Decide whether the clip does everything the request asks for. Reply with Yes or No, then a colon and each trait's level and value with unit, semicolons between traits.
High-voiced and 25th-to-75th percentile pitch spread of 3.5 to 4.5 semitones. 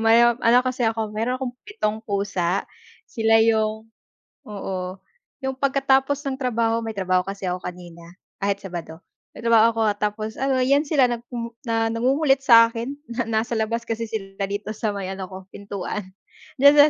Yes: high, 225 Hz; average, 3.8 semitones